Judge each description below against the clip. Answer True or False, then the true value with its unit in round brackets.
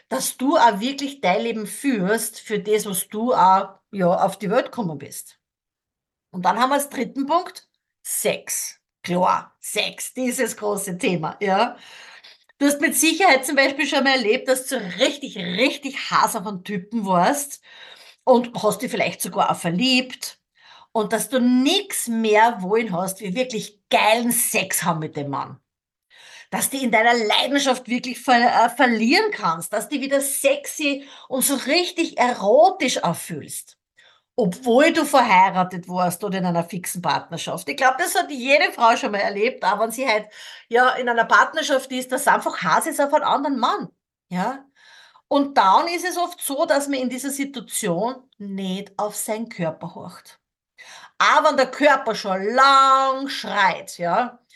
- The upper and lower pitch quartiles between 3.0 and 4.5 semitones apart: False (5.2 semitones)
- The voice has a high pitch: True (240 Hz)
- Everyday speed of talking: True (165 wpm)